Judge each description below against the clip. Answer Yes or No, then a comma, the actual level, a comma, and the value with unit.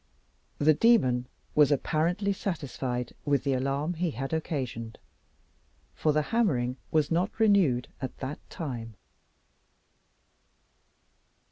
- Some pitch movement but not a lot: Yes, average, 5.0 semitones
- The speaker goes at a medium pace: No, slow, 105 wpm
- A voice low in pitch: No, medium, 145 Hz